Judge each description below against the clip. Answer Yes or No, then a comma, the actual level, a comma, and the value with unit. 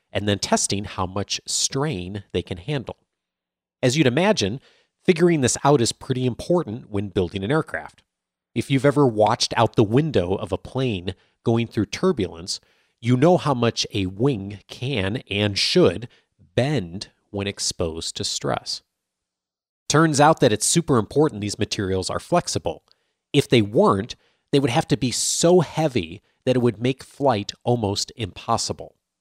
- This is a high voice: No, low, 115 Hz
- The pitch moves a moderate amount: No, wide, 6.2 semitones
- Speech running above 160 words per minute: No, average, 155 wpm